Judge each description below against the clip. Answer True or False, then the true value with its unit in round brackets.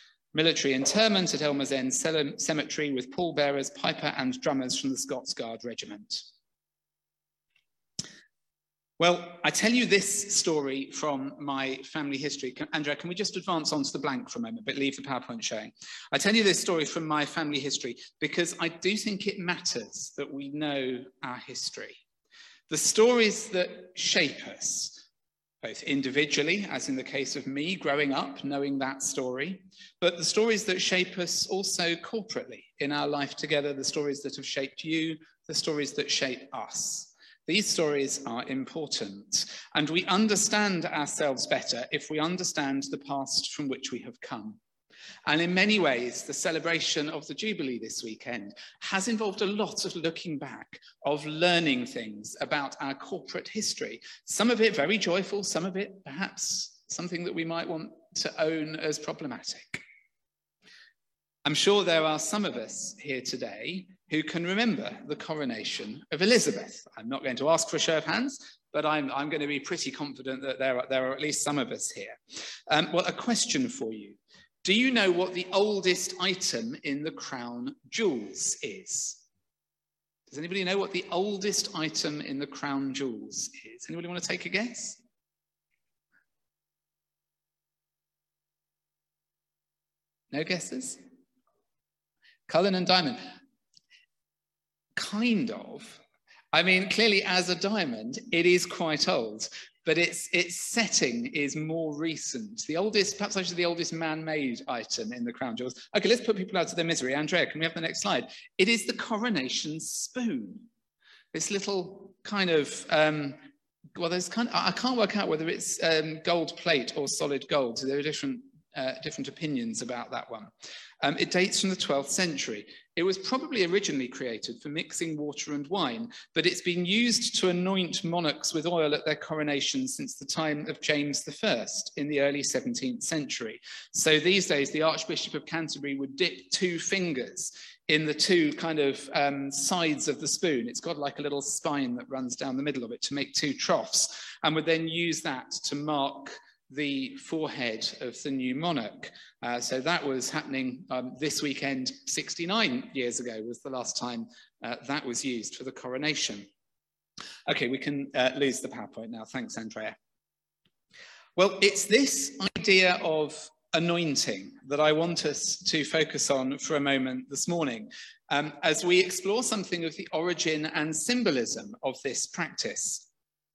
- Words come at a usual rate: True (170 wpm)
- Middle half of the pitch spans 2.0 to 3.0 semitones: False (5.5 semitones)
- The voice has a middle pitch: True (160 Hz)